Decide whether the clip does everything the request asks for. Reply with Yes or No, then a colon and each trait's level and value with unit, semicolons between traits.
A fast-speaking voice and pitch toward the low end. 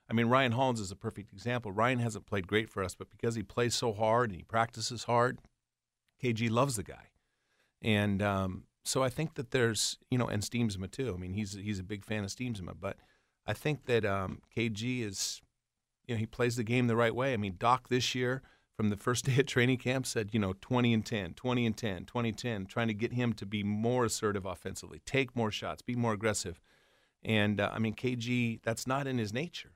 Yes: fast, 230 wpm; low, 115 Hz